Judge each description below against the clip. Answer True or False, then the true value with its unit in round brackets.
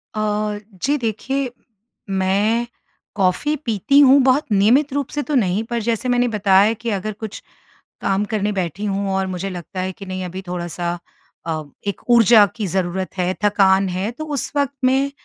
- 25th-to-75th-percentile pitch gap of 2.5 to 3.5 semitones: False (4.3 semitones)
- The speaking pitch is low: False (210 Hz)